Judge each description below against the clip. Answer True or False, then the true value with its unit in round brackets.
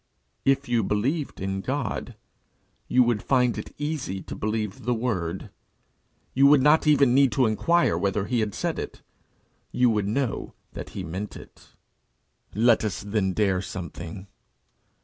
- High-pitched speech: False (115 Hz)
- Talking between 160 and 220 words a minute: False (150 wpm)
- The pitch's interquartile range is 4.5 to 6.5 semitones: True (5.1 semitones)